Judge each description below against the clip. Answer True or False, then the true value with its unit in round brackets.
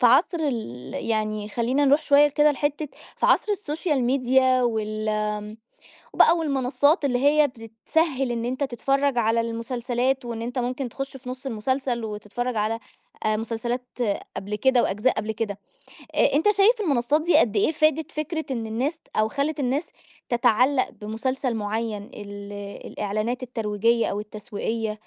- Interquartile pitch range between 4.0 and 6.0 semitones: True (4.3 semitones)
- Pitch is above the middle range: True (245 Hz)